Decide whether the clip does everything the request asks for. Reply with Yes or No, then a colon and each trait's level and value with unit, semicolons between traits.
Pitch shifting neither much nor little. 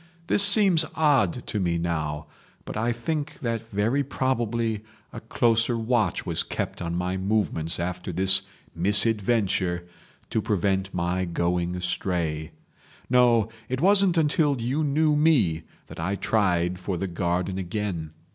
No: wide, 5.7 semitones